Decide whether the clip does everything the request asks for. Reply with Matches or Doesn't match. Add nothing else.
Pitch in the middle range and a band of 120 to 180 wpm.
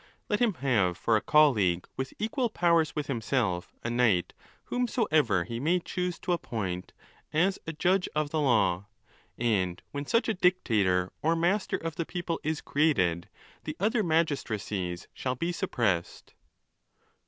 Matches